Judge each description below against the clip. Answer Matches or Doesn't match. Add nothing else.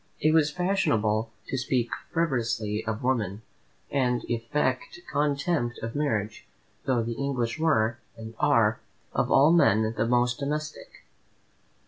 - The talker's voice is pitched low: Matches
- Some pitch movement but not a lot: Matches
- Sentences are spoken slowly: Matches